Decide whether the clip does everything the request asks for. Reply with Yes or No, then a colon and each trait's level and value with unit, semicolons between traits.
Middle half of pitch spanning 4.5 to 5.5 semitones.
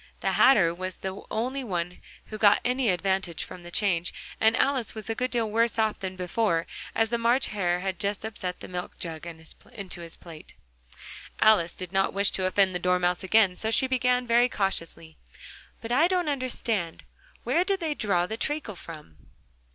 Yes: average, 4.8 semitones